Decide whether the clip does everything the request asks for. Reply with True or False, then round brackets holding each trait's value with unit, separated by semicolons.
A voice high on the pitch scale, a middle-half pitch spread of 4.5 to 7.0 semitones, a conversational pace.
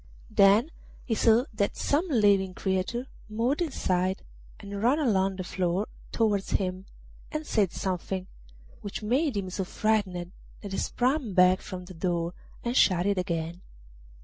False (200 Hz; 3.6 semitones; 150 wpm)